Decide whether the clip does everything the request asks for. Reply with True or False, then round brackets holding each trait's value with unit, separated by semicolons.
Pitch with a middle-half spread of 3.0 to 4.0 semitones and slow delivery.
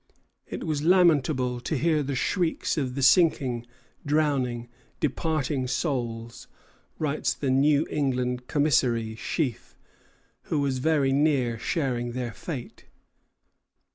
True (3.5 semitones; 110 wpm)